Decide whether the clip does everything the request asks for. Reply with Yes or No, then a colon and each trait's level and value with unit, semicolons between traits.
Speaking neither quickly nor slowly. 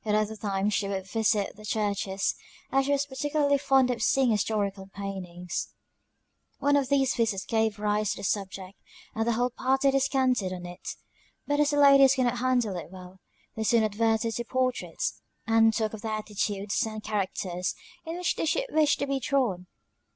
Yes: average, 185 wpm